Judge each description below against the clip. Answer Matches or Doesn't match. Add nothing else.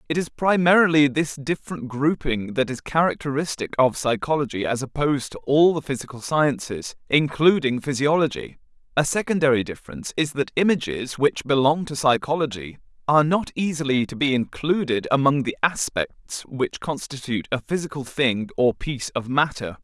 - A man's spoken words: Matches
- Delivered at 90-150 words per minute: Matches